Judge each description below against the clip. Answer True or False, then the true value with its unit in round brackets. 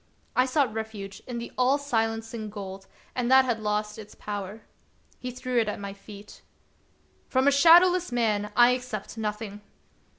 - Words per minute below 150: False (165 wpm)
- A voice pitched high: True (225 Hz)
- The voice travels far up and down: False (3.3 semitones)